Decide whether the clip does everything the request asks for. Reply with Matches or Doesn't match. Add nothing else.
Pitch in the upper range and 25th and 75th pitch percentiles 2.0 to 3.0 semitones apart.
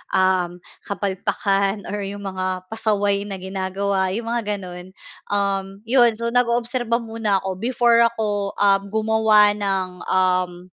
Matches